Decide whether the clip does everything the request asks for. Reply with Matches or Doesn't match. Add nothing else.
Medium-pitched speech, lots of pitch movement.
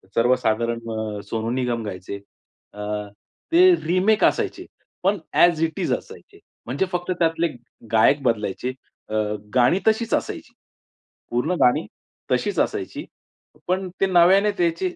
Matches